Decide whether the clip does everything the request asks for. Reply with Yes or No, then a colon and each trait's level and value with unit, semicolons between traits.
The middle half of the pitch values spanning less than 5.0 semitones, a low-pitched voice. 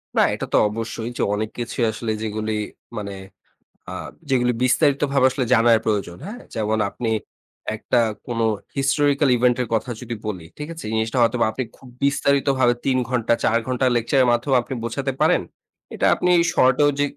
Yes: average, 3.3 semitones; low, 120 Hz